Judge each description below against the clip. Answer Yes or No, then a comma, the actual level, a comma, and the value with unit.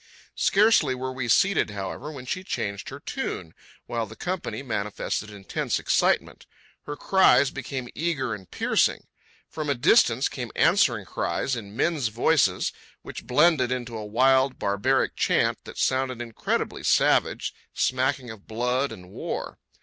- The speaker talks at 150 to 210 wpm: No, average, 140 wpm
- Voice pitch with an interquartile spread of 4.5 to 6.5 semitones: No, average, 4.1 semitones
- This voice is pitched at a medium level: No, low, 130 Hz